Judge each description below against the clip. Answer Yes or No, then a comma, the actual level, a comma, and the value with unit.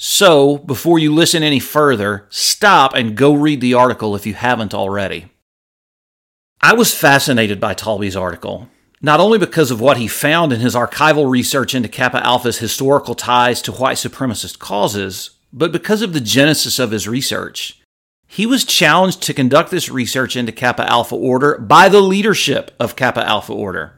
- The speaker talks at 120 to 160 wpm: No, average, 170 wpm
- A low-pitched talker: Yes, low, 130 Hz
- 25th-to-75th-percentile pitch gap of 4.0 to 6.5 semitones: Yes, average, 4.3 semitones